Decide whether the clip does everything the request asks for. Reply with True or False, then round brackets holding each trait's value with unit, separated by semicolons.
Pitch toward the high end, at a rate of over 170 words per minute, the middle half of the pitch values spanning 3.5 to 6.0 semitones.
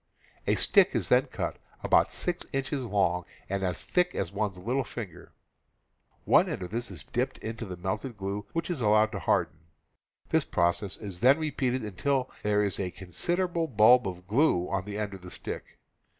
False (105 Hz; 185 wpm; 5.6 semitones)